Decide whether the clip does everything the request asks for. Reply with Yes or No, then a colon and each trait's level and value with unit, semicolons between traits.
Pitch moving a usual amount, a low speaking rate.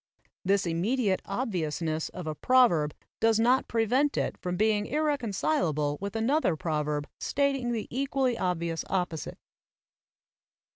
No: wide, 7.5 semitones; slow, 125 wpm